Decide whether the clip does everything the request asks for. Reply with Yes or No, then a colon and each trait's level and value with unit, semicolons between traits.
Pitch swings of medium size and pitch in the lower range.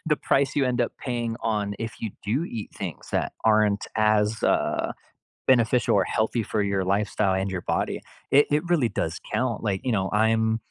Yes: average, 3.0 semitones; low, 110 Hz